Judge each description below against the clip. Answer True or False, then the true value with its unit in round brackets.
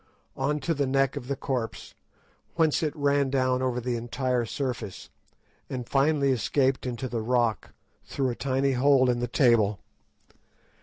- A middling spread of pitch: False (2.3 semitones)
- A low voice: True (130 Hz)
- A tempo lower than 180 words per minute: True (160 wpm)